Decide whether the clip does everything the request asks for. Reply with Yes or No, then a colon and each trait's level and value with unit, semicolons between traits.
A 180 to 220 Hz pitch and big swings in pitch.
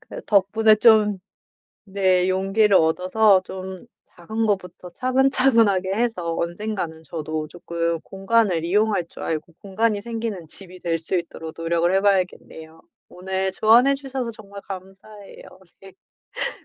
No: high, 190 Hz; average, 3.9 semitones